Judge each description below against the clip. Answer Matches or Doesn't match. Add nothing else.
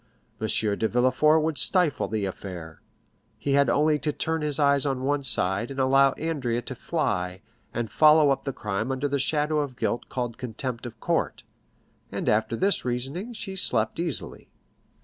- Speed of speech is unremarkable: Matches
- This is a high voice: Doesn't match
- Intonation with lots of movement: Doesn't match